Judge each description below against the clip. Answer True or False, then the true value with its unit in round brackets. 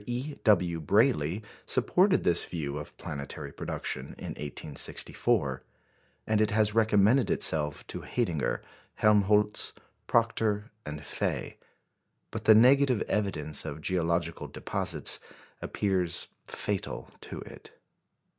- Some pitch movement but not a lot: False (5.8 semitones)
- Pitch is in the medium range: False (100 Hz)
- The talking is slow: True (110 wpm)